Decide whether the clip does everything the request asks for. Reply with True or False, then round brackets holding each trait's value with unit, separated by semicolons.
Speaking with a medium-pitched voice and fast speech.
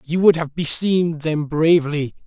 False (155 Hz; 160 wpm)